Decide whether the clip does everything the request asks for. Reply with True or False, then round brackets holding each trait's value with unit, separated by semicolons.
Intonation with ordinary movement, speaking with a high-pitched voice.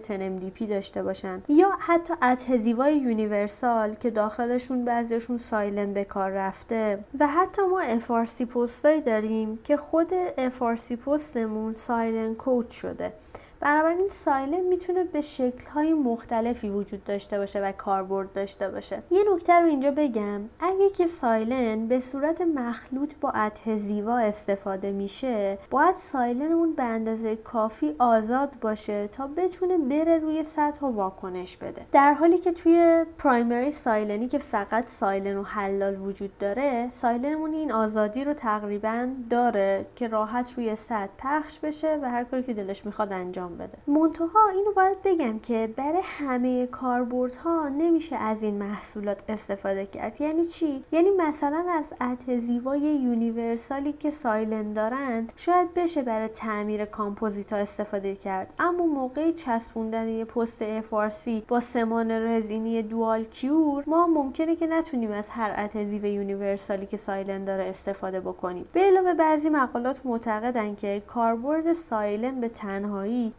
False (5.7 semitones; 235 Hz)